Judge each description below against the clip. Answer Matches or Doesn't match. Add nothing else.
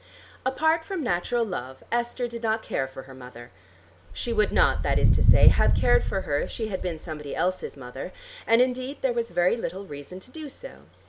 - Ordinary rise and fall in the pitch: Doesn't match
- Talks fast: Matches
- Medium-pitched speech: Doesn't match